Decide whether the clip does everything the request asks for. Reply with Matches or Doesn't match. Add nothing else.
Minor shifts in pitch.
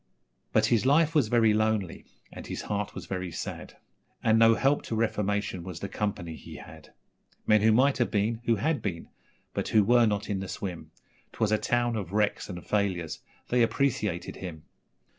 Doesn't match